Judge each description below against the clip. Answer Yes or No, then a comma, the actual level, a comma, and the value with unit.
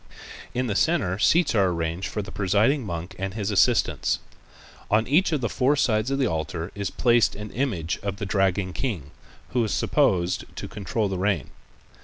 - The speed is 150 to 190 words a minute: Yes, average, 185 wpm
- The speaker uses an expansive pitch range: No, average, 4.5 semitones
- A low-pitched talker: Yes, low, 100 Hz